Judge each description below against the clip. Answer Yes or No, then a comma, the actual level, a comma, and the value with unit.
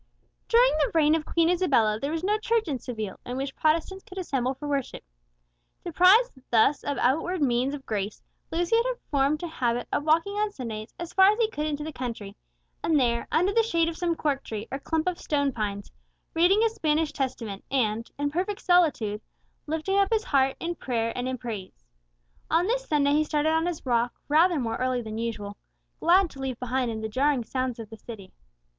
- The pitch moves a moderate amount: No, wide, 6.2 semitones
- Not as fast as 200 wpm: No, fast, 205 wpm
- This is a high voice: Yes, very high, 290 Hz